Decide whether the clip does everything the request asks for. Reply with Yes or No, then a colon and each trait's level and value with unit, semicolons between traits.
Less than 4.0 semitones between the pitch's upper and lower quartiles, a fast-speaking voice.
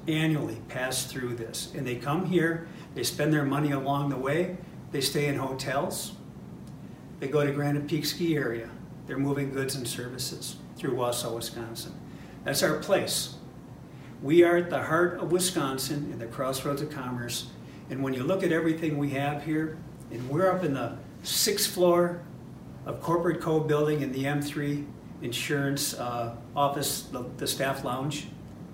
No: average, 3.3 semitones; average, 165 wpm